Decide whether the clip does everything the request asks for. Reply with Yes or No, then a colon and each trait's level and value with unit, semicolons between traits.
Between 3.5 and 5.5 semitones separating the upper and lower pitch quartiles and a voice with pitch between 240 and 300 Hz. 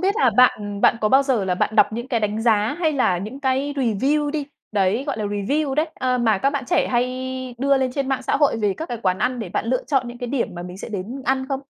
Yes: average, 4.5 semitones; very high, 250 Hz